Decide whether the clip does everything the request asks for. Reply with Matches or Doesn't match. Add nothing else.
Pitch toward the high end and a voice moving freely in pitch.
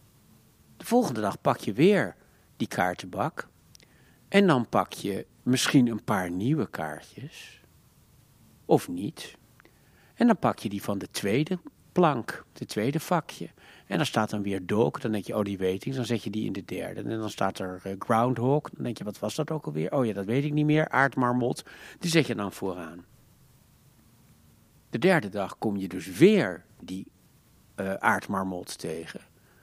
Doesn't match